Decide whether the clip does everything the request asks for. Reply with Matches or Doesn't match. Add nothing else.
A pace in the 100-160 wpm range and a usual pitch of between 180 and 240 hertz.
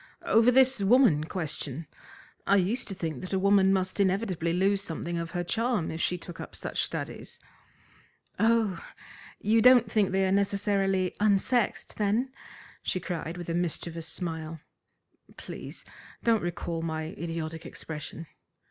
Matches